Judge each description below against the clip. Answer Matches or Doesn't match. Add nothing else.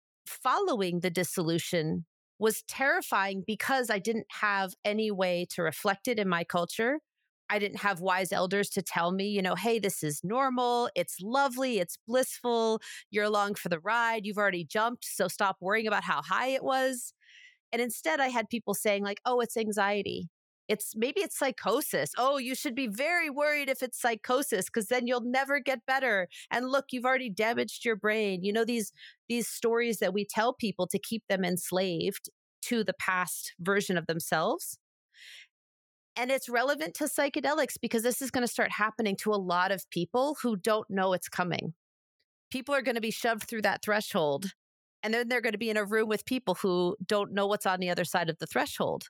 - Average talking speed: Matches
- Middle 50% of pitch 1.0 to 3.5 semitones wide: Doesn't match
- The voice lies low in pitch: Doesn't match